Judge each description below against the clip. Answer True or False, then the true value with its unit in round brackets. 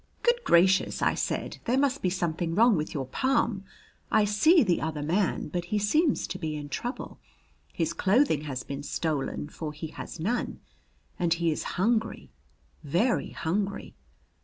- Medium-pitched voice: True (180 Hz)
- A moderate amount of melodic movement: False (6.0 semitones)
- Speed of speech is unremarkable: True (160 wpm)